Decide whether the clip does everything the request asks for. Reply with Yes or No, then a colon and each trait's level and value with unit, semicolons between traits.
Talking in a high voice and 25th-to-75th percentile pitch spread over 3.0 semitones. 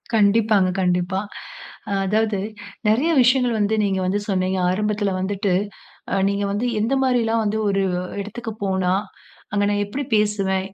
No: high, 205 Hz; narrow, 2.5 semitones